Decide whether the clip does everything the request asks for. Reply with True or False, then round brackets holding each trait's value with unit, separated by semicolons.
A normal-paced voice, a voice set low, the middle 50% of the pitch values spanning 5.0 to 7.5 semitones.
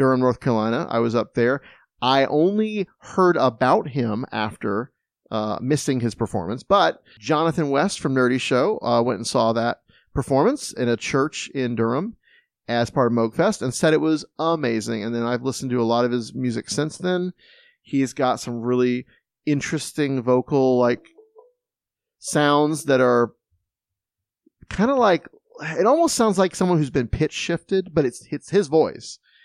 True (165 wpm; 130 Hz; 5.3 semitones)